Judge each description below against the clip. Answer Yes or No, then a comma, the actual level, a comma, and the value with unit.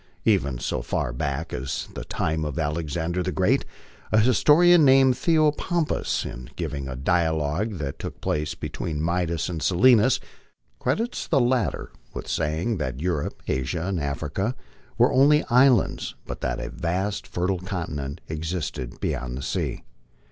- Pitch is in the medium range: No, very low, 85 Hz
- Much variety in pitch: Yes, wide, 7.8 semitones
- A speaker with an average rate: Yes, average, 150 wpm